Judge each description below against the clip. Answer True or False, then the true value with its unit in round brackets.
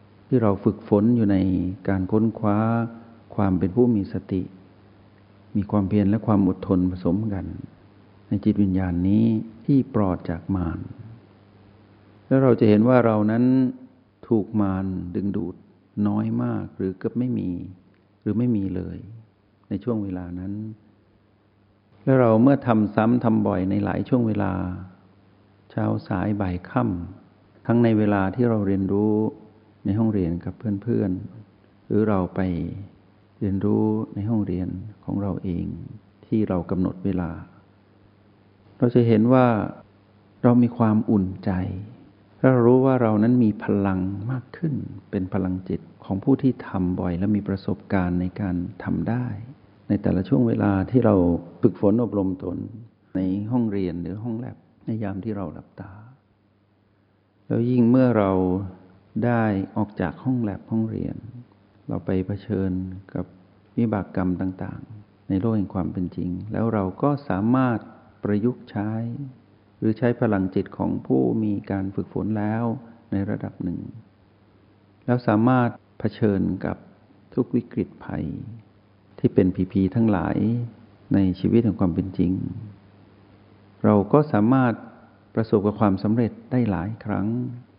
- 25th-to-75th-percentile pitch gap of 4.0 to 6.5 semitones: False (2.8 semitones)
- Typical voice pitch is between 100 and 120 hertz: True (105 Hz)